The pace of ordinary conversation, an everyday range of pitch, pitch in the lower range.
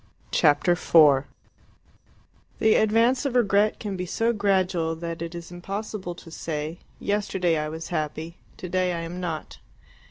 No: average, 145 wpm; average, 3.6 semitones; medium, 175 Hz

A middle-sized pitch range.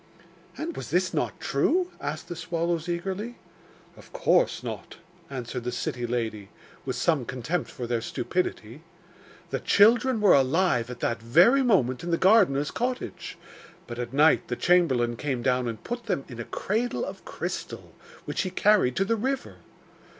No: wide, 8.7 semitones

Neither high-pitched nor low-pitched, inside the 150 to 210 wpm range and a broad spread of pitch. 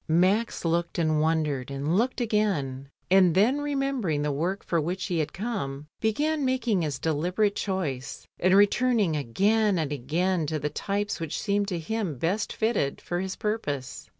Yes: medium, 180 Hz; average, 170 wpm; wide, 5.7 semitones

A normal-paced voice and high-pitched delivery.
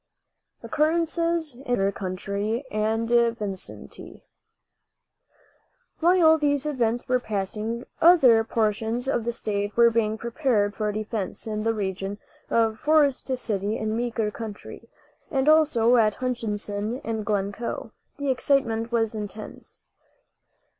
No: slow, 115 wpm; high, 225 Hz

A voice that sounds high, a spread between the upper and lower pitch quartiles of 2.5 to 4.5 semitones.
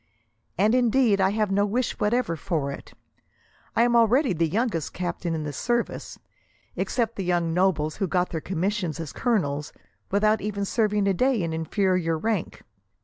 No: high, 195 Hz; average, 4.9 semitones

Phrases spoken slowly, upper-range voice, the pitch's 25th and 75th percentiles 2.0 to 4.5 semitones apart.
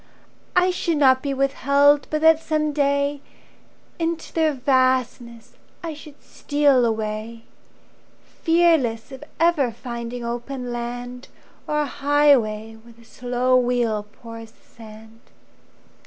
Yes: slow, 115 wpm; very high, 255 Hz; average, 3.8 semitones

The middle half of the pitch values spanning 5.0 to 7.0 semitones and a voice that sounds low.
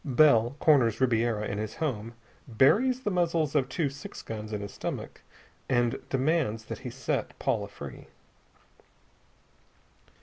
Yes: average, 5.3 semitones; low, 130 Hz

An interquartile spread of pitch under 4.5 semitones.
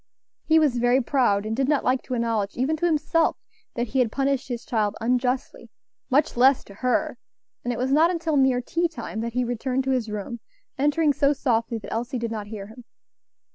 Yes: average, 3.3 semitones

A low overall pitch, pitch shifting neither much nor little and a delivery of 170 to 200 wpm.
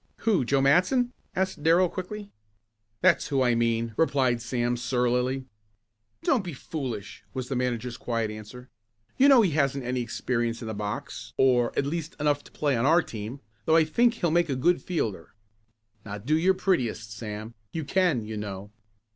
No: low, 130 Hz; wide, 6.1 semitones; average, 180 wpm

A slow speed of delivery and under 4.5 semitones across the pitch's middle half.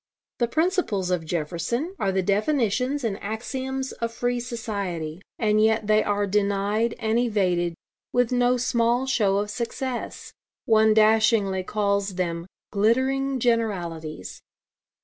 Yes: slow, 125 wpm; average, 3.8 semitones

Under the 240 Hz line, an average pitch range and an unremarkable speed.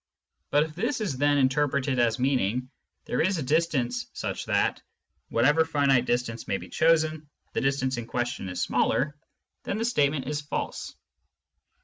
Yes: medium, 140 Hz; average, 3.9 semitones; average, 165 wpm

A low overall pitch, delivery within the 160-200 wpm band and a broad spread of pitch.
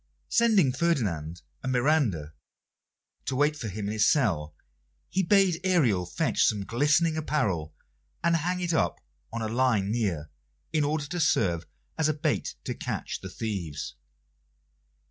No: low, 130 Hz; average, 145 wpm; wide, 8.5 semitones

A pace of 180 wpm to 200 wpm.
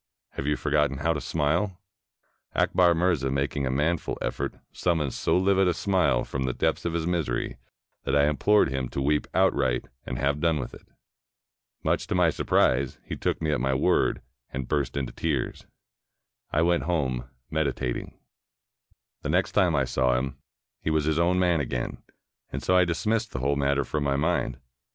Yes: average, 185 wpm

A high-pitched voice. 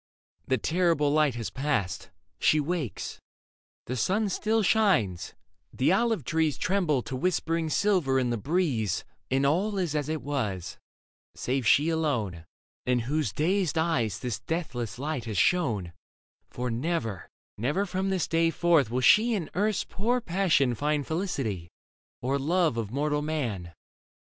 No: medium, 150 Hz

